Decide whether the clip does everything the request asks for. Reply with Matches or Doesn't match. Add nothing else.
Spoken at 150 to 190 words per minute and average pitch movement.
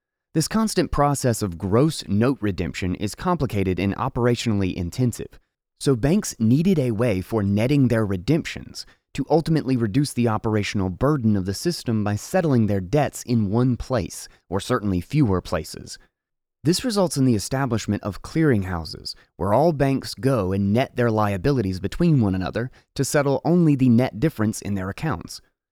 Doesn't match